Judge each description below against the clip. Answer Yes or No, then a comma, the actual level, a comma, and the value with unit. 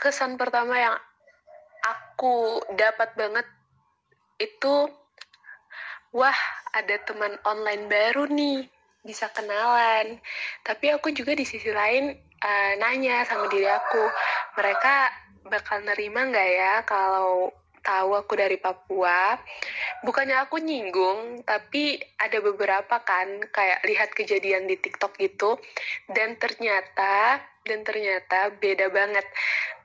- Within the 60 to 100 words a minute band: No, average, 110 wpm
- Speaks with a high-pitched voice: Yes, high, 220 Hz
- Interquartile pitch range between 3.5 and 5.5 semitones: Yes, average, 4.0 semitones